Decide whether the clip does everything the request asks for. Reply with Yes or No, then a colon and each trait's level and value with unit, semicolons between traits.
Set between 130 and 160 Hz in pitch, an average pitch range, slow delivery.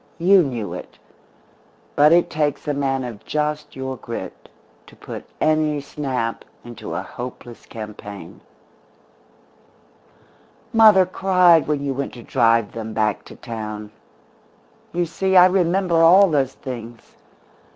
No: medium, 140 Hz; wide, 6.6 semitones; slow, 130 wpm